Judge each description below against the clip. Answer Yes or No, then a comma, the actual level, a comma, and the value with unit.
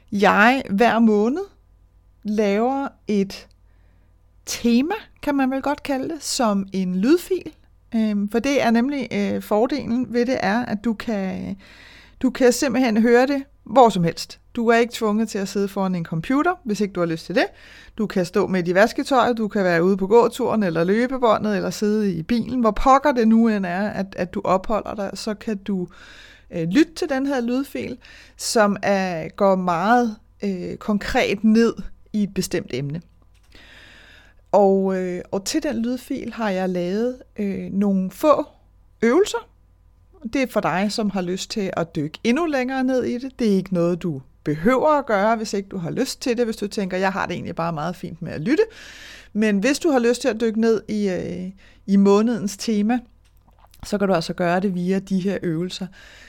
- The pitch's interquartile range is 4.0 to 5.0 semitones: Yes, average, 4.5 semitones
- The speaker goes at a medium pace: Yes, average, 190 wpm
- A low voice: No, high, 210 Hz